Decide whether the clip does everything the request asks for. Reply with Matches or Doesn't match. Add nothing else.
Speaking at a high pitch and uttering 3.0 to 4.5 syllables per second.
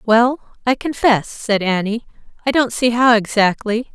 Matches